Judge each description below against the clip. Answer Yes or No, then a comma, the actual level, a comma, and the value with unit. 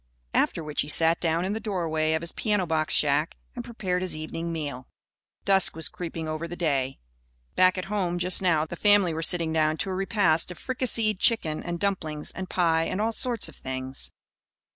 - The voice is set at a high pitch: No, medium, 170 Hz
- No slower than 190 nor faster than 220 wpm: Yes, average, 200 wpm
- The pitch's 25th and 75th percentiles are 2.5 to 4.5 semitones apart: Yes, average, 3.5 semitones